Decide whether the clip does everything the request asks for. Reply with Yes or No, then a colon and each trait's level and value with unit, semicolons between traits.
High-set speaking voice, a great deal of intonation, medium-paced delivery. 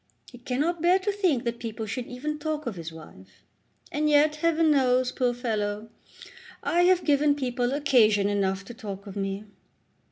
Yes: very high, 250 Hz; wide, 6.4 semitones; average, 170 wpm